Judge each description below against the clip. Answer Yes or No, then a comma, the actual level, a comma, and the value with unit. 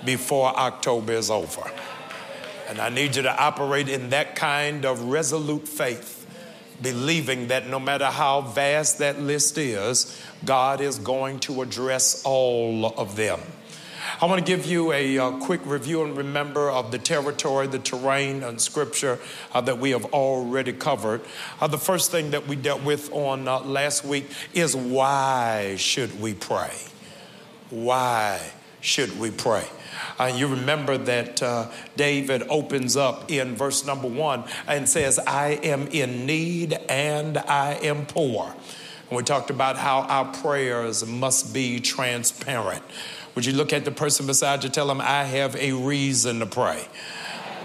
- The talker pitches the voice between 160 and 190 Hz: No, low, 135 Hz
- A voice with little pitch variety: Yes, narrow, 2.2 semitones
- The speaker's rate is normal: Yes, average, 160 wpm